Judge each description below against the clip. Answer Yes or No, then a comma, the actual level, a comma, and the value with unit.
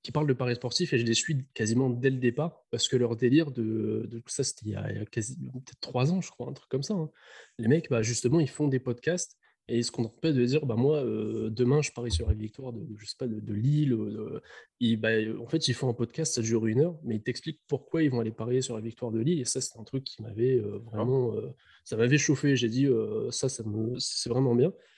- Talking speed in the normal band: No, fast, 270 wpm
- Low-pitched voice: Yes, low, 125 Hz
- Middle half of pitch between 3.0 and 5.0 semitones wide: Yes, average, 3.4 semitones